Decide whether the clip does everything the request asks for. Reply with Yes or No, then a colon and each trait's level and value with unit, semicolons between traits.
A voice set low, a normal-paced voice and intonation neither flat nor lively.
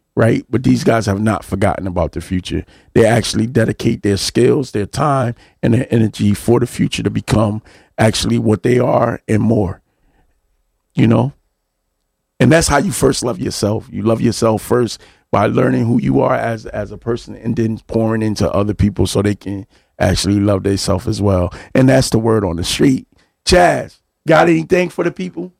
Yes: low, 110 Hz; average, 190 wpm; average, 3.2 semitones